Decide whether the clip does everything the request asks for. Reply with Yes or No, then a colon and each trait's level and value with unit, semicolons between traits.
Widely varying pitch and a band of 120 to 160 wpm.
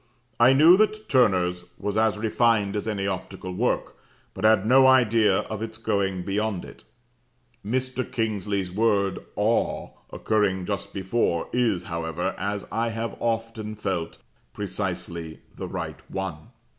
No: average, 3.1 semitones; slow, 135 wpm